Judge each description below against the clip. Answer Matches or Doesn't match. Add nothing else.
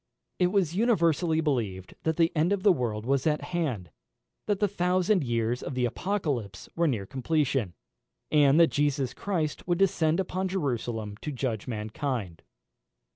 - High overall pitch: Doesn't match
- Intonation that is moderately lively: Doesn't match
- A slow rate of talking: Doesn't match